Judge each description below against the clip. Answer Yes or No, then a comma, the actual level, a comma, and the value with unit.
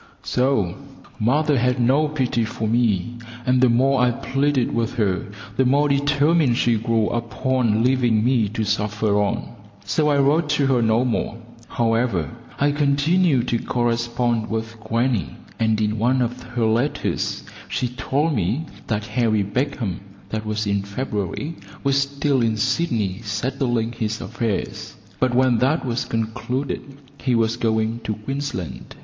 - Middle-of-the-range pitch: No, low, 120 Hz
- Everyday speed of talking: Yes, average, 150 wpm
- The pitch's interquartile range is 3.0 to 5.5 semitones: Yes, average, 3.4 semitones